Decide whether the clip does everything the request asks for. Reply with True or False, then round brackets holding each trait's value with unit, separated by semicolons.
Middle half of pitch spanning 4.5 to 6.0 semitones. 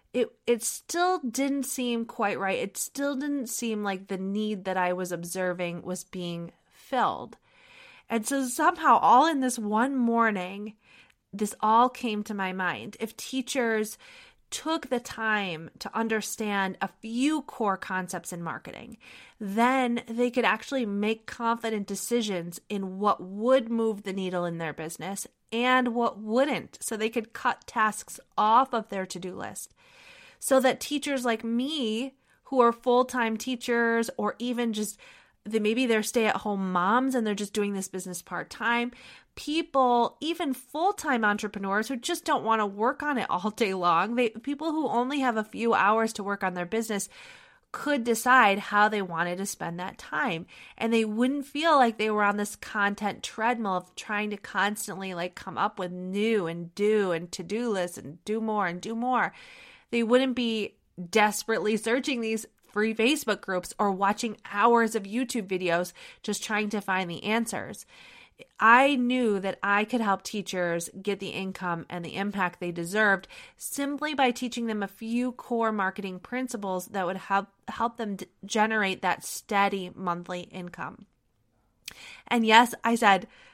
False (4.0 semitones)